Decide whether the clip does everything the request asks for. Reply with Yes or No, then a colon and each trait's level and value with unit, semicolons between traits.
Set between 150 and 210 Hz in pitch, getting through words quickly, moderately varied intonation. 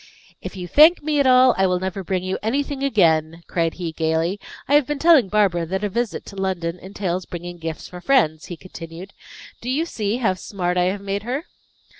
No: high, 190 Hz; fast, 210 wpm; wide, 5.8 semitones